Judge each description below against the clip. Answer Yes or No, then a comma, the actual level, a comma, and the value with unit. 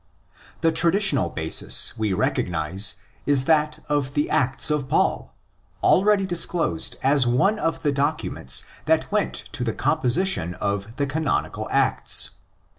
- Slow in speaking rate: Yes, slow, 125 wpm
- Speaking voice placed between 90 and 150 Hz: Yes, medium, 140 Hz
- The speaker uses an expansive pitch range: Yes, wide, 6.2 semitones